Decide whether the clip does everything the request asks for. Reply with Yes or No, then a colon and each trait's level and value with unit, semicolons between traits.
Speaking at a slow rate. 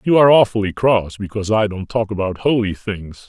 No: average, 200 wpm